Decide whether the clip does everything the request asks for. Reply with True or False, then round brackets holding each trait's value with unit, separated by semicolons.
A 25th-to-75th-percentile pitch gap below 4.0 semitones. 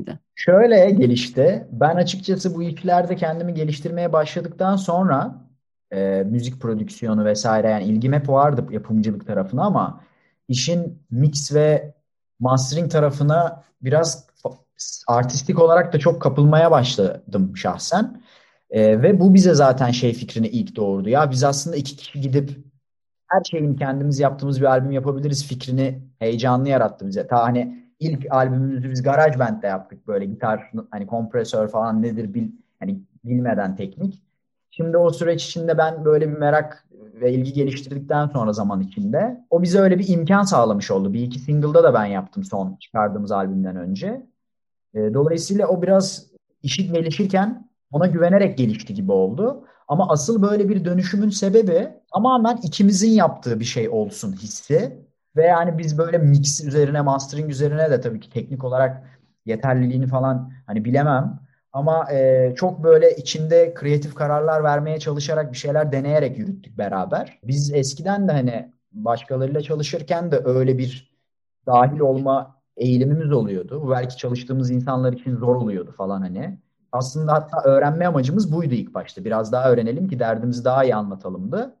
False (5.4 semitones)